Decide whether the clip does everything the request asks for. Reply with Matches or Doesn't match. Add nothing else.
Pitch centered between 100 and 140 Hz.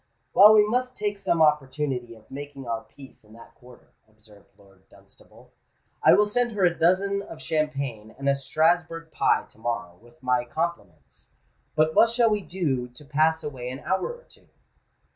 Doesn't match